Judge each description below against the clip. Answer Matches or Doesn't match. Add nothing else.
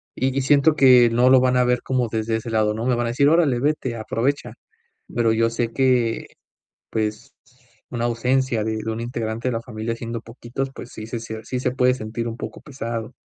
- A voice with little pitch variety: Matches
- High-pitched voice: Doesn't match